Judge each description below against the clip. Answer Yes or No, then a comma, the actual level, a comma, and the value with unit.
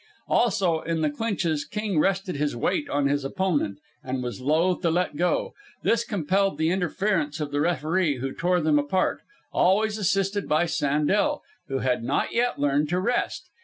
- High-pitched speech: No, medium, 170 Hz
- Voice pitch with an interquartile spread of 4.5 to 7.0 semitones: Yes, average, 5.1 semitones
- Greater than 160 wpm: Yes, average, 170 wpm